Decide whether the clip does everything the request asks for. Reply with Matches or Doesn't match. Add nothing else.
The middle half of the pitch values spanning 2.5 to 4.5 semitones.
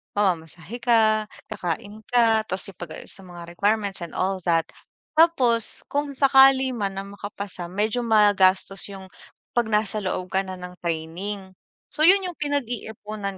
Matches